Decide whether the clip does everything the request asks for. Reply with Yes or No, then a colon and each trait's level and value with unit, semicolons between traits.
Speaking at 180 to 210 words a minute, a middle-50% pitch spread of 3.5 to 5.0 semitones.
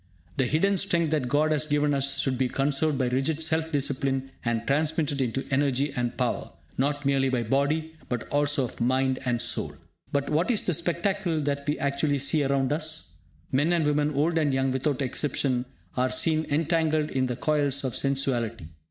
No: average, 185 wpm; average, 2.8 semitones